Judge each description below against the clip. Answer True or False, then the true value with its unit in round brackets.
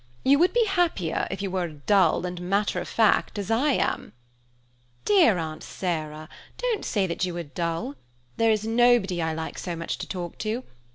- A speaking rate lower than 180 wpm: False (190 wpm)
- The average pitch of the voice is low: False (190 Hz)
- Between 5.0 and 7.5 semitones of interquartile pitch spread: True (5.3 semitones)